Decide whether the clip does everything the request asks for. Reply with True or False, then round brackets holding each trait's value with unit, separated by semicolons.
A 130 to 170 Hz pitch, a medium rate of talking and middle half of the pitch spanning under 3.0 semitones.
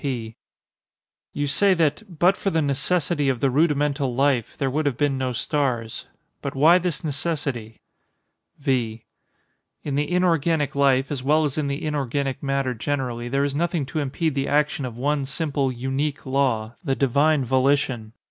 True (140 Hz; 160 wpm; 2.4 semitones)